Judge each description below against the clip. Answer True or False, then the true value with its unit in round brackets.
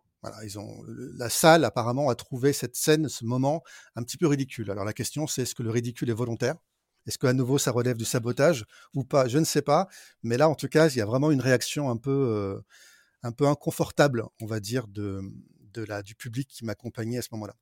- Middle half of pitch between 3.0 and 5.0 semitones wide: True (3.9 semitones)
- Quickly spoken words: True (240 wpm)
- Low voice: True (125 Hz)